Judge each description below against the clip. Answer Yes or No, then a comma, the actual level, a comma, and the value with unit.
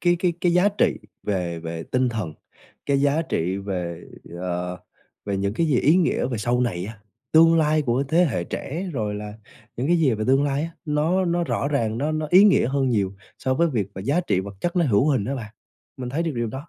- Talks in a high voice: No, low, 130 Hz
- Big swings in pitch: Yes, wide, 7.6 semitones